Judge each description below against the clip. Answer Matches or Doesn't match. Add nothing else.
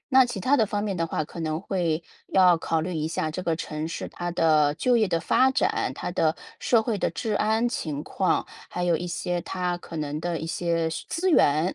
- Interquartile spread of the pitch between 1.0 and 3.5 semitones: Doesn't match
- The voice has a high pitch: Doesn't match